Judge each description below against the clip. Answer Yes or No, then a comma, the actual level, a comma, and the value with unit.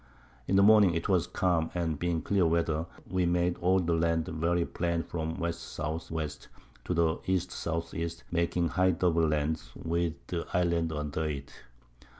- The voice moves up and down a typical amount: No, narrow, 1.4 semitones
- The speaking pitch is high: No, very low, 85 Hz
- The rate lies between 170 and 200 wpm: No, average, 160 wpm